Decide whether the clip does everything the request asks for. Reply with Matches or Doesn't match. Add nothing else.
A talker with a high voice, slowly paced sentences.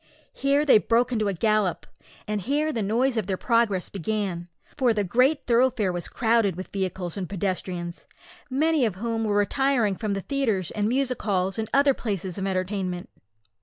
Doesn't match